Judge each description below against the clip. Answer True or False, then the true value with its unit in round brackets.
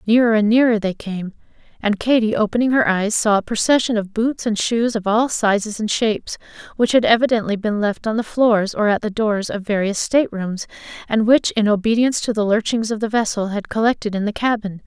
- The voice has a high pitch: True (220 Hz)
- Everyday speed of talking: False (210 wpm)